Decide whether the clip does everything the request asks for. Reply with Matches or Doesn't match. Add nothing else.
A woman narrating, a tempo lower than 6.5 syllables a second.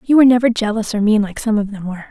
Doesn't match